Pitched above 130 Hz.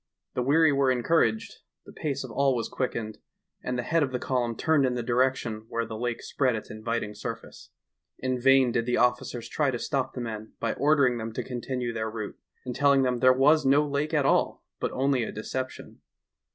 No: low, 125 Hz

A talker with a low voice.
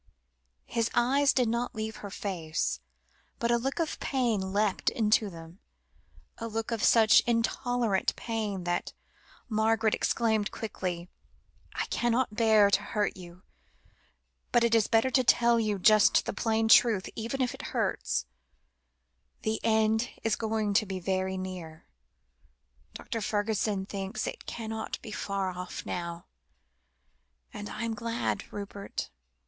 No: high, 220 Hz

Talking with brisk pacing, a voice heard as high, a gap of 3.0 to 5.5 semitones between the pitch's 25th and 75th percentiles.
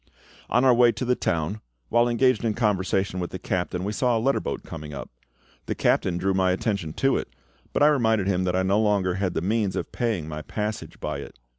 No: fast, 230 wpm; low, 100 Hz; average, 4.2 semitones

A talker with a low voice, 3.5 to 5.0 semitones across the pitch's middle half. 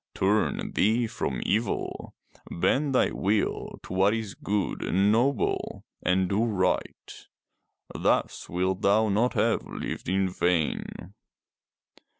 No: low, 100 Hz; average, 3.0 semitones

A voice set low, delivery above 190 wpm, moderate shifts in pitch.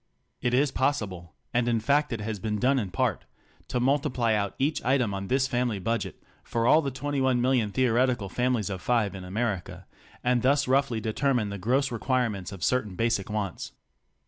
Yes: low, 120 Hz; average, 200 wpm; average, 3.9 semitones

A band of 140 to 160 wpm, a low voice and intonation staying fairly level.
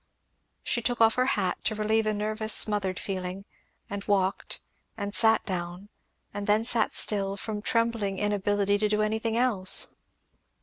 No: average, 150 wpm; high, 210 Hz; narrow, 2.0 semitones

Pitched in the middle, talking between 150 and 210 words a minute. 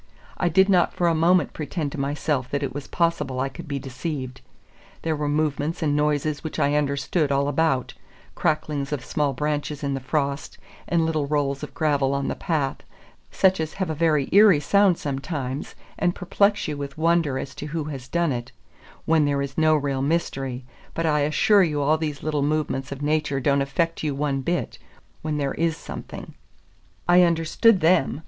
Yes: medium, 150 Hz; average, 190 wpm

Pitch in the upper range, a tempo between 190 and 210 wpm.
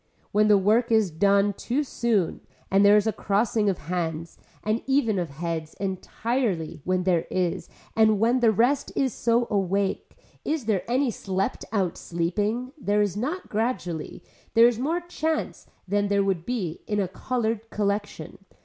No: high, 205 Hz; average, 165 wpm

